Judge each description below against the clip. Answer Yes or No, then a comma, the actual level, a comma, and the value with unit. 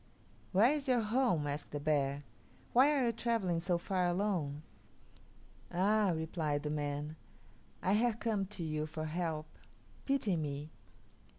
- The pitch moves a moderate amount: No, wide, 6.0 semitones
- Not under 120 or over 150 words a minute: Yes, average, 140 wpm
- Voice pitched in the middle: Yes, medium, 175 Hz